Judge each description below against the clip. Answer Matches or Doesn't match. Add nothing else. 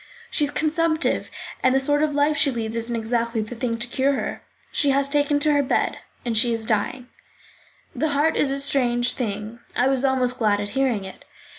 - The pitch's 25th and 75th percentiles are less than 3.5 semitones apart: Doesn't match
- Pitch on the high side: Matches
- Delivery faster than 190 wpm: Matches